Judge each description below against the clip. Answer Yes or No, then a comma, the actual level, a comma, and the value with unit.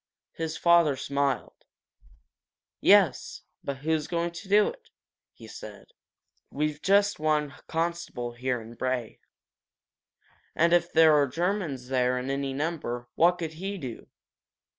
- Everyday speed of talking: No, slow, 130 wpm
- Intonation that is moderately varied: Yes, average, 4.5 semitones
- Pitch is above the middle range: No, medium, 155 Hz